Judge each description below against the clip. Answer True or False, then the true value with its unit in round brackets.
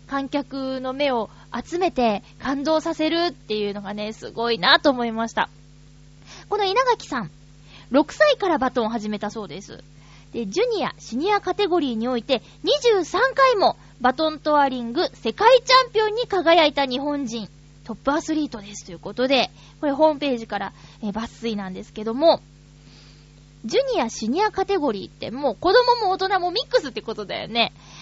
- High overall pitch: True (260 Hz)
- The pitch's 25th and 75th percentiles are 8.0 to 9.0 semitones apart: True (8.3 semitones)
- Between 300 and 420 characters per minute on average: True (350 characters per minute)